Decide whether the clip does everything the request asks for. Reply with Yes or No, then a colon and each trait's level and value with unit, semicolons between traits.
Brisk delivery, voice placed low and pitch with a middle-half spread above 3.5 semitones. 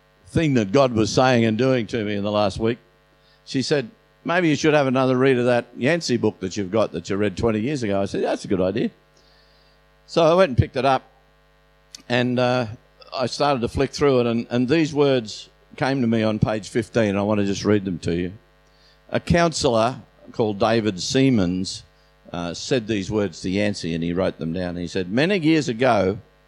Yes: fast, 215 wpm; low, 115 Hz; average, 4.7 semitones